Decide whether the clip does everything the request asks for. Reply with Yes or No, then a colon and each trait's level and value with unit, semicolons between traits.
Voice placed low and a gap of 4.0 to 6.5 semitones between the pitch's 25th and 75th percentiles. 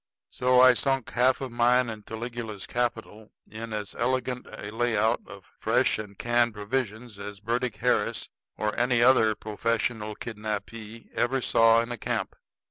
No: low, 115 Hz; narrow, 2.4 semitones